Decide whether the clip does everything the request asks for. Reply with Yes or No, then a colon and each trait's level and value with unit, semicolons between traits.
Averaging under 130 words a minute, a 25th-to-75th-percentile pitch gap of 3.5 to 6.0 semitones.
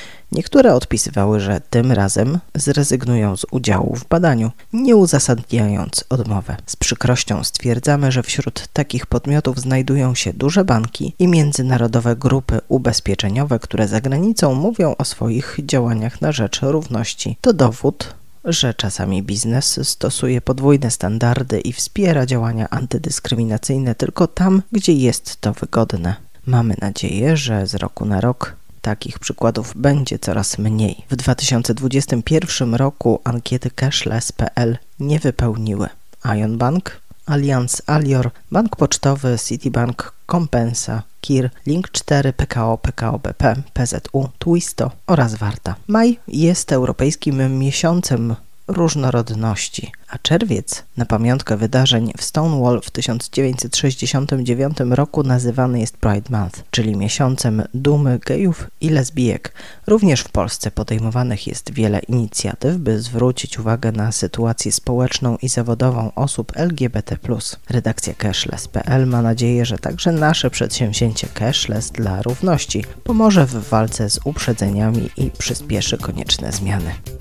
Yes: average, 120 wpm; average, 3.9 semitones